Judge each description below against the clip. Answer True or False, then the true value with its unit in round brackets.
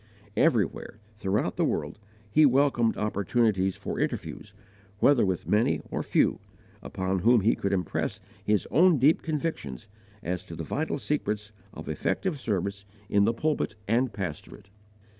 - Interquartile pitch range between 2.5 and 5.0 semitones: False (5.5 semitones)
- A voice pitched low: True (105 Hz)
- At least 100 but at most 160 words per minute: True (140 wpm)